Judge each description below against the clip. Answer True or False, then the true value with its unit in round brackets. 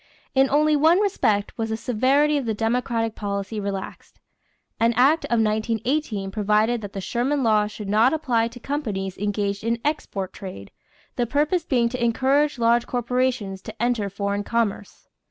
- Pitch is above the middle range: True (230 Hz)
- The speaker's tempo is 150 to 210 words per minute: True (160 wpm)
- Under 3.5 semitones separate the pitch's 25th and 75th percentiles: False (4.0 semitones)